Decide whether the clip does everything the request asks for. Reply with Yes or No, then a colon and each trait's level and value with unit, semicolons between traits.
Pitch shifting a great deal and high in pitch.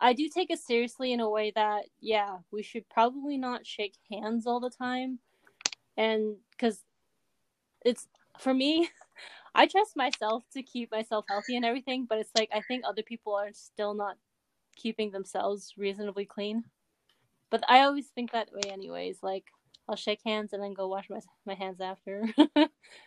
No: average, 3.4 semitones; high, 220 Hz